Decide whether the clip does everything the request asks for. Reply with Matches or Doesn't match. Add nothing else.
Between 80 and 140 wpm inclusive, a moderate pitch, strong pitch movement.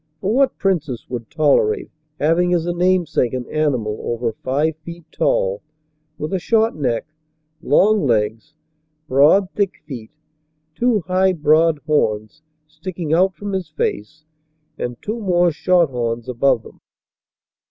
Matches